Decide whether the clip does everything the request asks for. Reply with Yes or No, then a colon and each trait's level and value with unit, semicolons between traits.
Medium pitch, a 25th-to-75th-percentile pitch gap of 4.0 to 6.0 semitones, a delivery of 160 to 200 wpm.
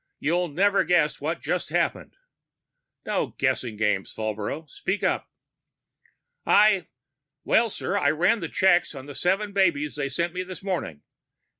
No: medium, 170 Hz; average, 5.2 semitones; average, 145 wpm